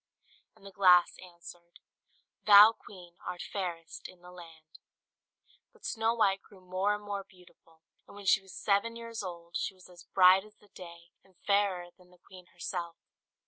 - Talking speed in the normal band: Yes, average, 175 wpm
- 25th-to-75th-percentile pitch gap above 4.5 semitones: No, narrow, 2.4 semitones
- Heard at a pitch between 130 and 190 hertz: Yes, medium, 185 Hz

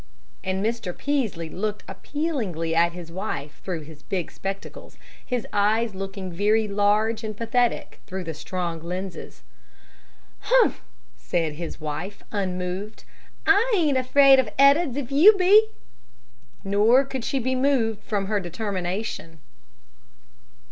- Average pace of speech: No, slow, 125 wpm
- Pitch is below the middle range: No, high, 205 Hz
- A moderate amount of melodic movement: No, wide, 6.0 semitones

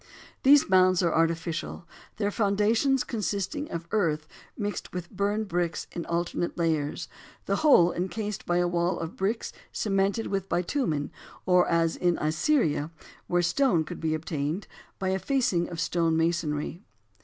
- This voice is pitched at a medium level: Yes, medium, 175 Hz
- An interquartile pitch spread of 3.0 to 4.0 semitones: Yes, average, 3.6 semitones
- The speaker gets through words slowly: No, average, 145 wpm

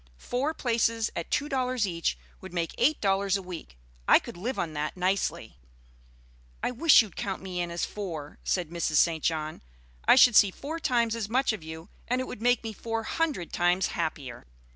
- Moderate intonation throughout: No, wide, 6.2 semitones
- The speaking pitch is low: No, high, 195 Hz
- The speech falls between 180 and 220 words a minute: Yes, average, 195 wpm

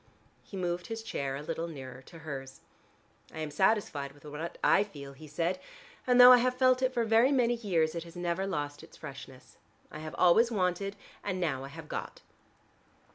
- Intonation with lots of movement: Yes, wide, 6.9 semitones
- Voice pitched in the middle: Yes, medium, 170 Hz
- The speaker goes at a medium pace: Yes, average, 195 wpm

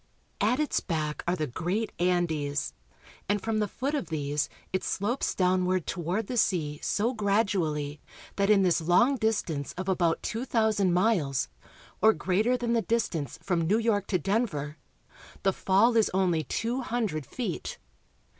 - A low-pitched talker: No, high, 190 Hz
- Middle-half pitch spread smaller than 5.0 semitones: No, average, 5.3 semitones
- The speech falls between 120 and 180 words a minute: Yes, average, 160 wpm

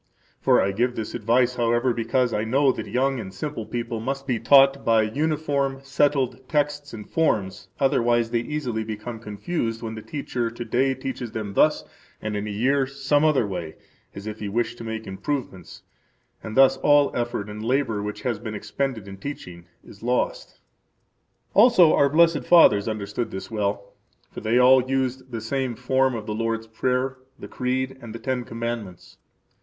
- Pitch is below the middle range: Yes, low, 120 Hz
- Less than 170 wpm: No, average, 180 wpm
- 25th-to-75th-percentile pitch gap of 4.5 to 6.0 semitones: No, average, 3.6 semitones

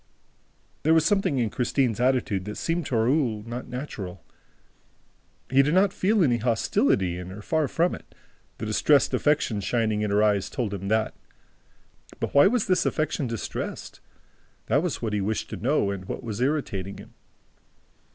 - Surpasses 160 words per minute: Yes, average, 170 wpm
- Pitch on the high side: No, low, 120 Hz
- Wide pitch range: Yes, wide, 6.1 semitones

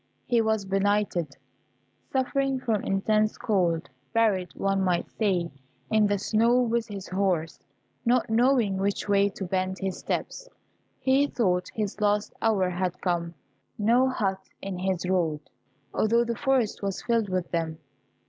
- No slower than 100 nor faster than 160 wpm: Yes, average, 145 wpm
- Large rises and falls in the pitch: No, average, 3.6 semitones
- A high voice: Yes, high, 200 Hz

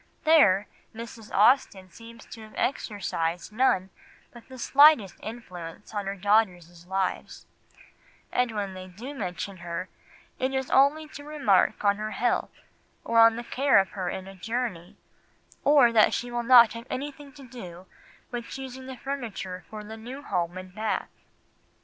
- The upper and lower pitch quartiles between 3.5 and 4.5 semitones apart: No, average, 5.3 semitones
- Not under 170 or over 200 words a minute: No, average, 155 wpm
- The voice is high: Yes, high, 220 Hz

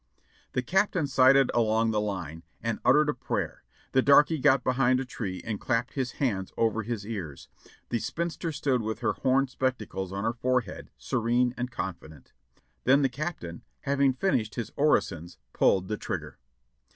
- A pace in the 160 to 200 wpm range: Yes, average, 165 wpm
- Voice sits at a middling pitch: No, low, 125 Hz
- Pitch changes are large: No, average, 4.1 semitones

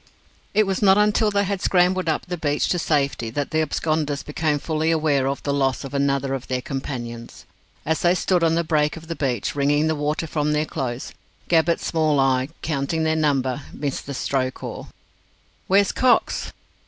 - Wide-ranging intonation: No, average, 3.1 semitones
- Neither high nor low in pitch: Yes, medium, 150 Hz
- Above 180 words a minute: Yes, average, 190 wpm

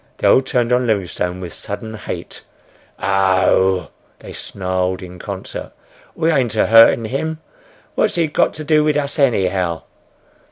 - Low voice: Yes, low, 110 Hz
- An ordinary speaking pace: Yes, average, 160 wpm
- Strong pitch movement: Yes, wide, 6.6 semitones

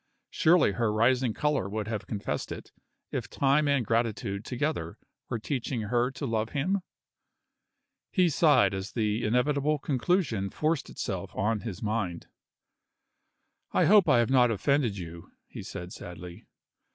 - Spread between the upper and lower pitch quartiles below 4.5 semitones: No, wide, 5.4 semitones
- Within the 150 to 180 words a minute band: No, average, 140 wpm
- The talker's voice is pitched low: Yes, low, 120 Hz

